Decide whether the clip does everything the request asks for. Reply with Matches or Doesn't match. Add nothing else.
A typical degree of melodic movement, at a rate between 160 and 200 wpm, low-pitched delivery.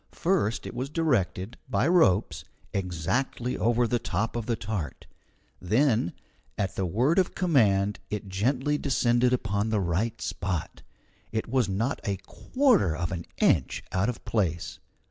Doesn't match